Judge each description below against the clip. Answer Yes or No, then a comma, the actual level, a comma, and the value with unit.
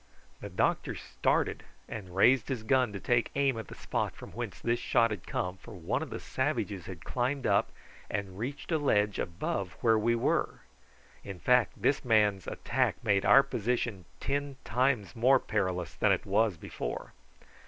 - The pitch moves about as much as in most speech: Yes, average, 4.7 semitones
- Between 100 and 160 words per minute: No, average, 175 wpm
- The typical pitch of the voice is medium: No, low, 110 Hz